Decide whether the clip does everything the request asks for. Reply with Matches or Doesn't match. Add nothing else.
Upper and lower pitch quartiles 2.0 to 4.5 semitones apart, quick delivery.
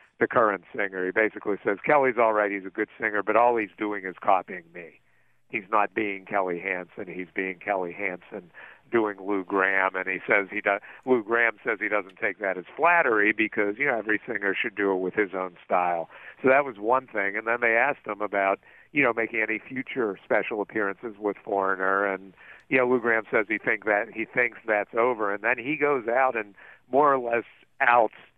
Matches